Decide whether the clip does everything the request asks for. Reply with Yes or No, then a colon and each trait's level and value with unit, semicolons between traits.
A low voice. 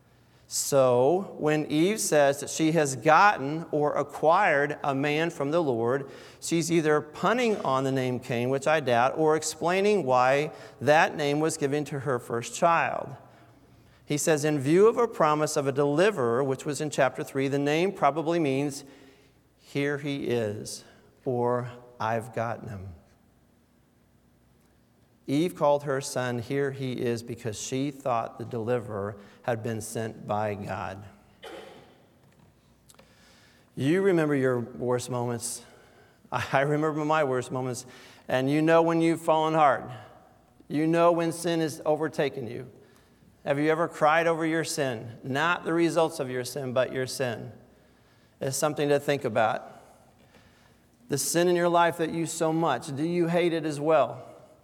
No: medium, 145 Hz